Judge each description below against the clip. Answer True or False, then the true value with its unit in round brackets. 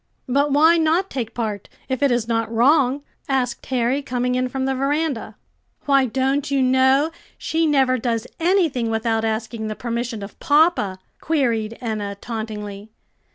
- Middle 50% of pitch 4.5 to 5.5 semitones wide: False (3.8 semitones)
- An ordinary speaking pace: True (155 wpm)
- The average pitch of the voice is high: True (255 Hz)